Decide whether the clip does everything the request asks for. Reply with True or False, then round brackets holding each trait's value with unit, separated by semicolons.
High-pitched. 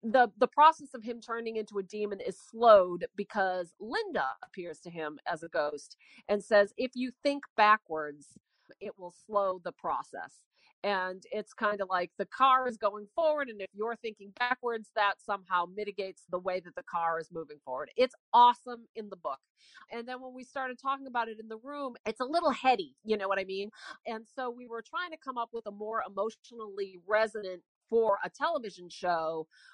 True (215 Hz)